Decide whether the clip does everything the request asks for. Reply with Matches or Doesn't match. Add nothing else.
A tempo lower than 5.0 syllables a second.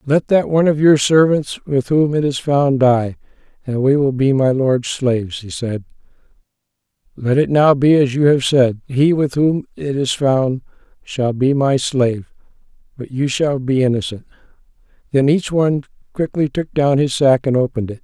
Matches